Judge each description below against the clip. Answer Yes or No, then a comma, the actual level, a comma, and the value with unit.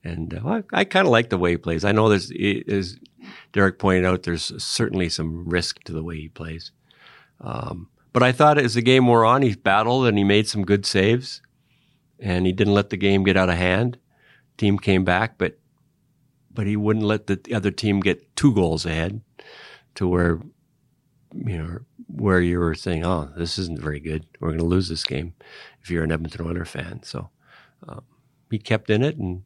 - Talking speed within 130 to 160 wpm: No, fast, 205 wpm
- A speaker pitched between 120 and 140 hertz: No, low, 100 Hz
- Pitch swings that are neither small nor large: No, wide, 6.4 semitones